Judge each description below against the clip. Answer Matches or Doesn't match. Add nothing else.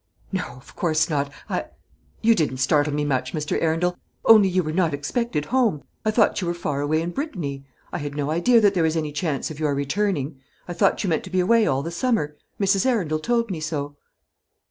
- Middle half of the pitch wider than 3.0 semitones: Matches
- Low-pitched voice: Doesn't match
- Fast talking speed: Matches